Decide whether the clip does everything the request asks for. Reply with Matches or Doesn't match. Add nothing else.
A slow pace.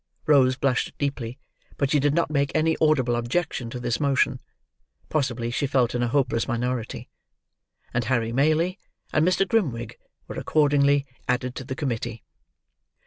Doesn't match